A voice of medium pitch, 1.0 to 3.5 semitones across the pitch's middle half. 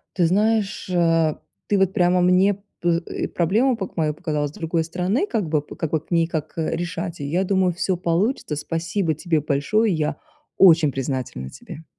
Yes: medium, 170 Hz; average, 3.2 semitones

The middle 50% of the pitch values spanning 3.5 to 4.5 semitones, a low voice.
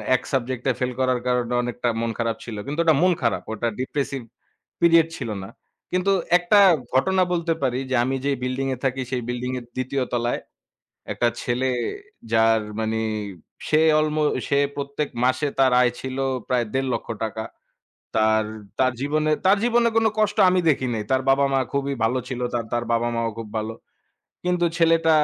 Yes: average, 4.1 semitones; low, 130 Hz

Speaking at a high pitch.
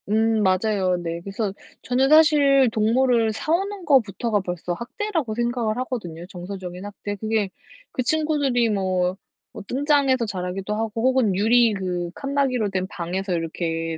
Yes: high, 215 Hz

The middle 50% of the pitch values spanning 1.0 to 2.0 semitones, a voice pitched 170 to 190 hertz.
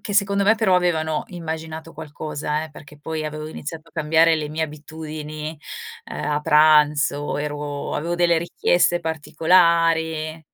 No: narrow, 1.6 semitones; medium, 160 Hz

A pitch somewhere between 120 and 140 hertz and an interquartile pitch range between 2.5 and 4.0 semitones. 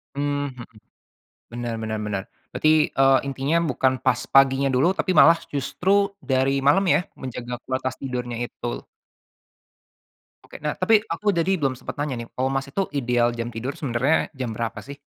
Yes: low, 135 Hz; average, 2.9 semitones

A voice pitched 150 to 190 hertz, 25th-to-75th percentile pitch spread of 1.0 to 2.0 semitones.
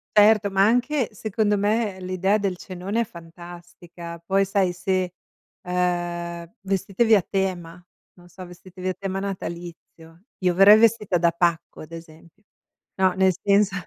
No: medium, 185 Hz; narrow, 2.4 semitones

